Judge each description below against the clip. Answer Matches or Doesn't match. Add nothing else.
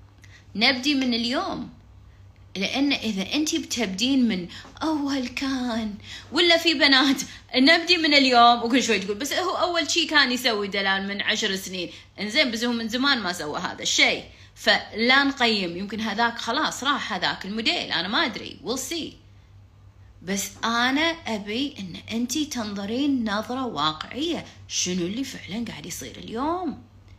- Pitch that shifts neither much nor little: Doesn't match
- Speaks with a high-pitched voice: Matches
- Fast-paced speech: Matches